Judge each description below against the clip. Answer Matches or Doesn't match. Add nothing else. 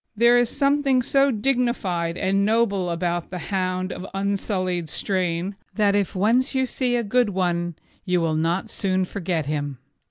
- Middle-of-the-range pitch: Doesn't match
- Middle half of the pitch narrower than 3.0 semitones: Doesn't match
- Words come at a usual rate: Matches